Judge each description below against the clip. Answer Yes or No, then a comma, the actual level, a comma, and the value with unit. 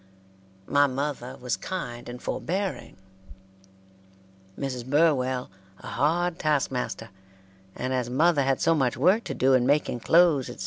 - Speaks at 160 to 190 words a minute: No, average, 140 wpm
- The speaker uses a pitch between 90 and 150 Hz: Yes, low, 135 Hz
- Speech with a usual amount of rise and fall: Yes, average, 4.2 semitones